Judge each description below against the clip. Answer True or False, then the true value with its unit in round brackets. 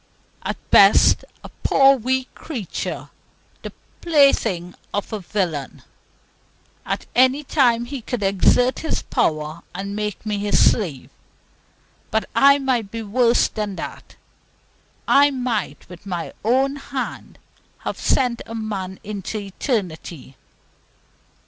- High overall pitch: True (220 Hz)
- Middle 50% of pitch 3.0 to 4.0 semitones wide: False (5.0 semitones)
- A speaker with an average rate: False (120 wpm)